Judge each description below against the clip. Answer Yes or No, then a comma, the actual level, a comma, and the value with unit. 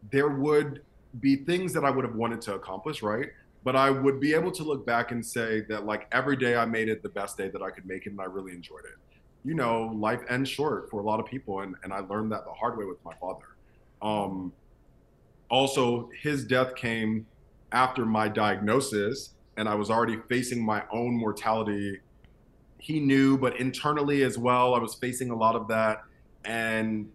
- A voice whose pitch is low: Yes, low, 115 Hz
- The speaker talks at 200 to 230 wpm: Yes, fast, 205 wpm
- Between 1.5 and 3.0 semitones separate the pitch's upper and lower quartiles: No, average, 3.7 semitones